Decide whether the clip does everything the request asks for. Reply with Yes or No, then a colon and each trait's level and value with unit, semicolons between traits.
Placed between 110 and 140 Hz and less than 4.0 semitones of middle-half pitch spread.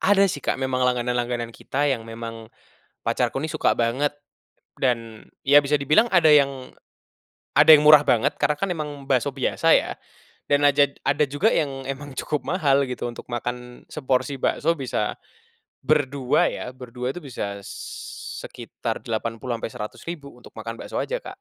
Yes: low, 135 Hz; average, 3.2 semitones